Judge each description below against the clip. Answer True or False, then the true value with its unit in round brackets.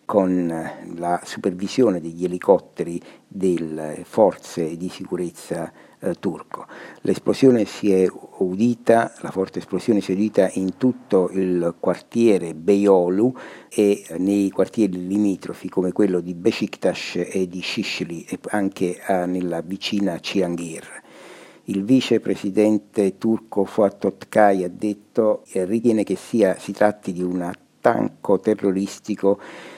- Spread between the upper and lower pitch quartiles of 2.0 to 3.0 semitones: True (2.6 semitones)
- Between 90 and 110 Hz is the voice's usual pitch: True (95 Hz)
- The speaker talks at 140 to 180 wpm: False (115 wpm)